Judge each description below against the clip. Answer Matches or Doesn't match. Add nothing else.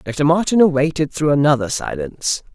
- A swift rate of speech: Doesn't match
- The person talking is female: Doesn't match